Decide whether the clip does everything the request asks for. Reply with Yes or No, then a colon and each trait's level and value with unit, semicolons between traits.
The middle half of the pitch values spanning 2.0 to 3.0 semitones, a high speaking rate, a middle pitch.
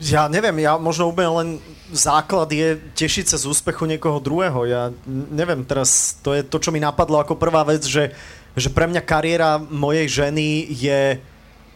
Yes: narrow, 2.4 semitones; fast, 175 wpm; medium, 155 Hz